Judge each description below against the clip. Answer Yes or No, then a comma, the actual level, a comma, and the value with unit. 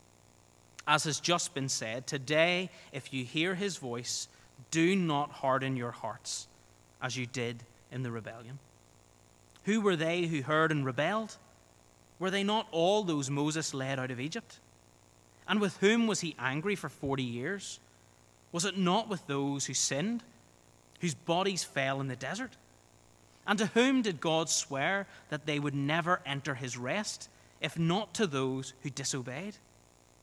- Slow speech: No, average, 160 wpm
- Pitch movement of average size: No, wide, 5.7 semitones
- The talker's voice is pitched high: No, medium, 145 Hz